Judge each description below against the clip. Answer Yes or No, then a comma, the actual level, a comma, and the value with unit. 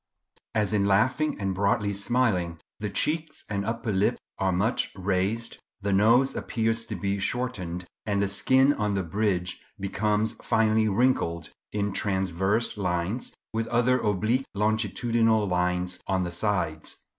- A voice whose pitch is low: Yes, low, 105 Hz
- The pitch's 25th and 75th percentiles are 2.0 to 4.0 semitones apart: Yes, average, 3.1 semitones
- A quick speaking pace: No, average, 140 wpm